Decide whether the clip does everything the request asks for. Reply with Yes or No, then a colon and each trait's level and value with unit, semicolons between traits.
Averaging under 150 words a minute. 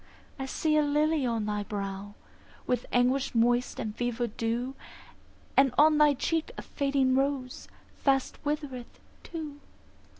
Yes: slow, 135 wpm